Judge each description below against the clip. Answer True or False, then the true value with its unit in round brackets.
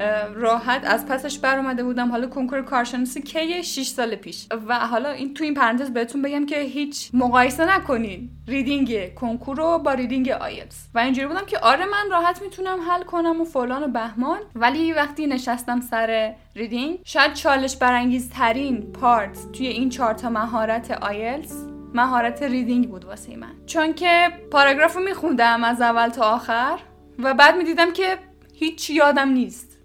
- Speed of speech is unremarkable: False (170 wpm)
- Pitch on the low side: False (260 Hz)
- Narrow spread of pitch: False (4.2 semitones)